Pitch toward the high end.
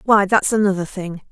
Yes: high, 195 Hz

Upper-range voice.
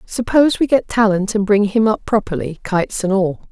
Yes: high, 205 Hz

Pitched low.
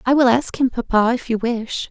No: high, 240 Hz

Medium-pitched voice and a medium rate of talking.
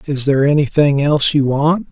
Yes: medium, 145 Hz; average, 190 wpm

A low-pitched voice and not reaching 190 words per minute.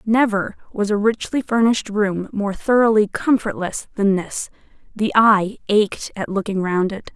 No: high, 210 Hz; average, 145 wpm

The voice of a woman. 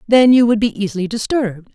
Yes: female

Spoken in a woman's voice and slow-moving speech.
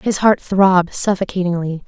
Yes: female; slow, 130 wpm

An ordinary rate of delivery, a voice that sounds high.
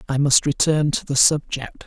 No: average, 195 wpm; medium, 140 Hz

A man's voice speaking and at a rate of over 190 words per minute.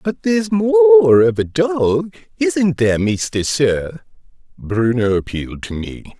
No: male; slow, 135 wpm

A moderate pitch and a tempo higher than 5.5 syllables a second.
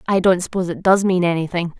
Yes: medium, 180 Hz; 6.8 syllables/s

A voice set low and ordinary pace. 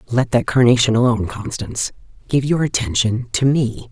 Yes: low, 120 Hz; average, 155 wpm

